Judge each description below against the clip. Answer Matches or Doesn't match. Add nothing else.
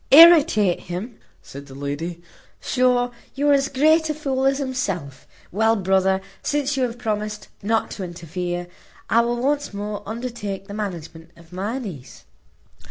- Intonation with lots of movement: Matches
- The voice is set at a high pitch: Matches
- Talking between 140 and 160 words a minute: Matches